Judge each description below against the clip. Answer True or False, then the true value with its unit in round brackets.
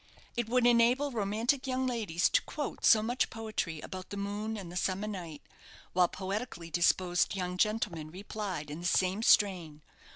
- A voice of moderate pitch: False (200 Hz)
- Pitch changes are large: False (4.2 semitones)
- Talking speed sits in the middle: True (165 wpm)